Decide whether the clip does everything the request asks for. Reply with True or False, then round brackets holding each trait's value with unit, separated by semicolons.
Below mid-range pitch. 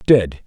True (100 Hz)